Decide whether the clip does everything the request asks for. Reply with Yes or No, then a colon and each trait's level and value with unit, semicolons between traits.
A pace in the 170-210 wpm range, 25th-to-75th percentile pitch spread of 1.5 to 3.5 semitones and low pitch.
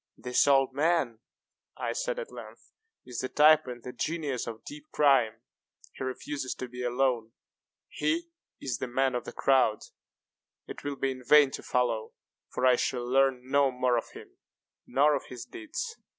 Yes: average, 175 wpm; average, 3.1 semitones; low, 130 Hz